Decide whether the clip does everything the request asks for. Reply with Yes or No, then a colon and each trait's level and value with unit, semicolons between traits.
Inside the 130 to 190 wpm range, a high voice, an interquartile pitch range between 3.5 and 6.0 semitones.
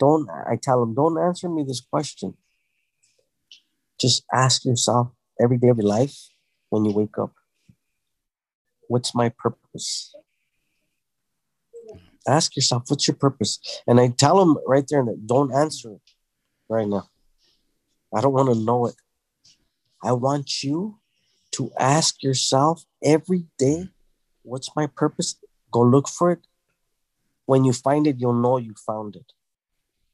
No: average, 140 wpm; low, 135 Hz; average, 4.0 semitones